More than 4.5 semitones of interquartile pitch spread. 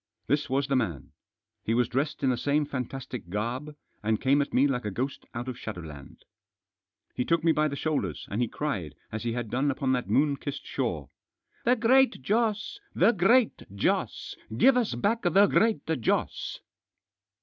Yes: average, 5.3 semitones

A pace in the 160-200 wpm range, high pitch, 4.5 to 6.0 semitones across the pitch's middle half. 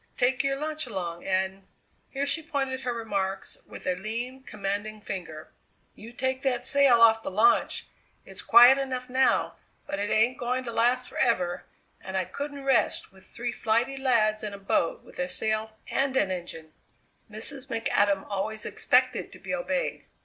Yes: average, 170 wpm; high, 230 Hz; average, 4.9 semitones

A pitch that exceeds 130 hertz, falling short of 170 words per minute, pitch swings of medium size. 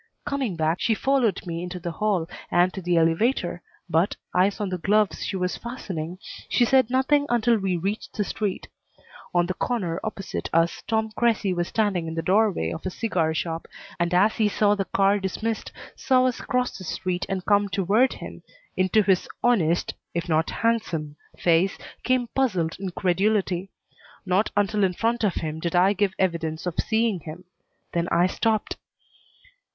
No: high, 190 Hz; average, 175 wpm; average, 4.0 semitones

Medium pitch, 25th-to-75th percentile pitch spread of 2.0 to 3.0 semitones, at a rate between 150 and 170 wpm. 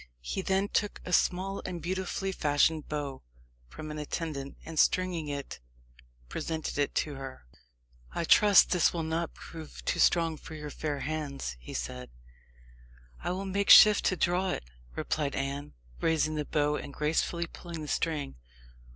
No: medium, 155 Hz; average, 3.5 semitones; average, 160 wpm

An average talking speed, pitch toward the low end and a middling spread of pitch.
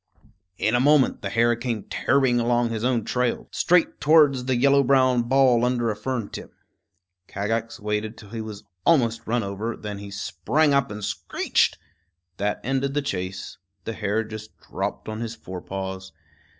Yes: average, 175 wpm; low, 115 Hz; average, 3.7 semitones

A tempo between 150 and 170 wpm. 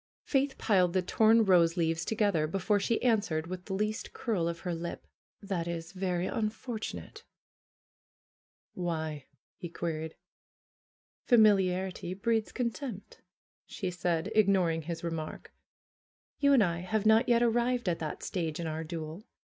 No: average, 140 wpm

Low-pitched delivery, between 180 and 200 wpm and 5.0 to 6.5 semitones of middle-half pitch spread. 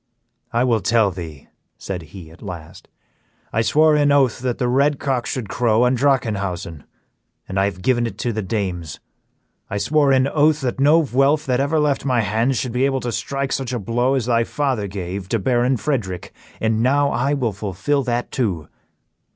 Yes: low, 120 Hz; average, 190 wpm; average, 5.3 semitones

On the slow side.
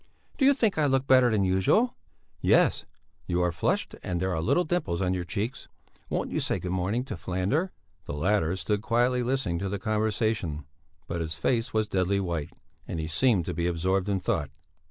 No: average, 195 wpm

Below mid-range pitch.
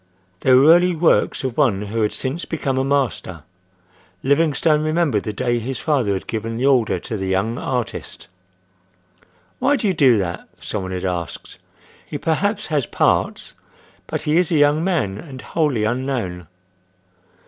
Yes: low, 130 Hz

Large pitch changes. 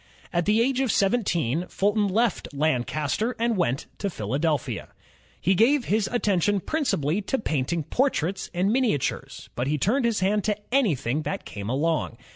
Yes: wide, 6.8 semitones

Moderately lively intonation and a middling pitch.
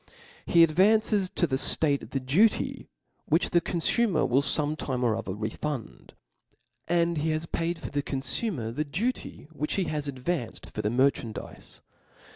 Yes: average, 4.5 semitones; medium, 150 Hz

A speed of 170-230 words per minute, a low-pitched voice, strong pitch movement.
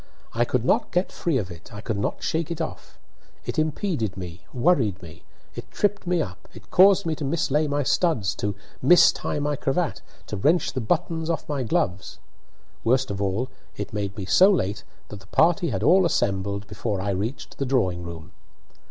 Yes: average, 190 wpm; low, 125 Hz; wide, 8.4 semitones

